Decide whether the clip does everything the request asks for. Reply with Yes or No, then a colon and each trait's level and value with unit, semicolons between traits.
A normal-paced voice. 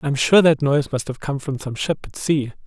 No: fast, 295 wpm